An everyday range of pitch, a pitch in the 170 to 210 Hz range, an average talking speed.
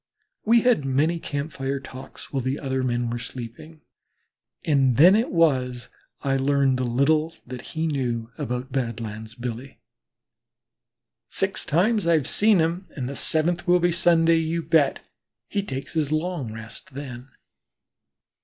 No: average, 4.6 semitones; medium, 140 Hz; average, 150 wpm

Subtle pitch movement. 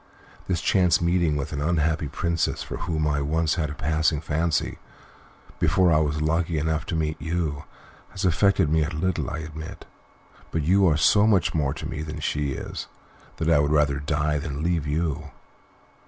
Yes: narrow, 2.0 semitones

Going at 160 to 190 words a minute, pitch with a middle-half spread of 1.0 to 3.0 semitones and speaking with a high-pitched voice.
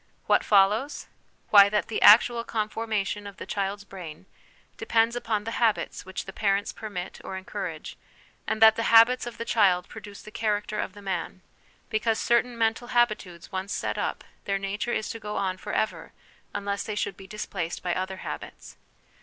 Yes: average, 180 wpm; narrow, 2.5 semitones; high, 205 Hz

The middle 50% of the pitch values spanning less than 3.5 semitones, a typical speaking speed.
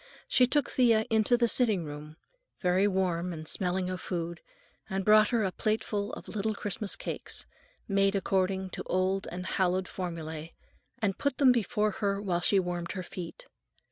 Yes: average, 3.1 semitones; average, 170 wpm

